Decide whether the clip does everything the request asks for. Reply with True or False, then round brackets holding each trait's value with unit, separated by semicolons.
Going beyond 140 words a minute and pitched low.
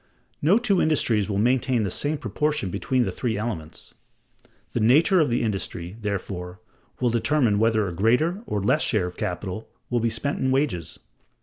True (180 wpm; 115 Hz)